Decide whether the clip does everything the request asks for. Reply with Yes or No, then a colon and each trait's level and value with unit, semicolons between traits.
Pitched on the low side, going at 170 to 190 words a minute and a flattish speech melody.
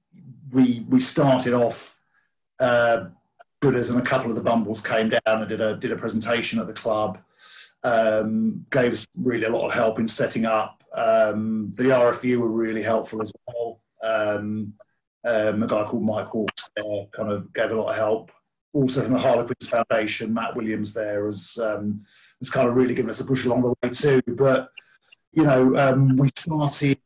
No: low, 115 Hz; average, 185 wpm; average, 3.0 semitones